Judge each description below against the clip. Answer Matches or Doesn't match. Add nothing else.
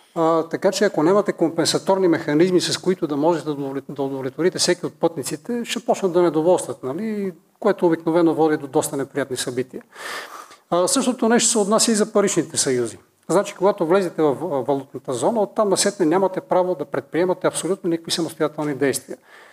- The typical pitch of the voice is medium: Matches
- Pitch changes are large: Doesn't match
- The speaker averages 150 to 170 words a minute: Matches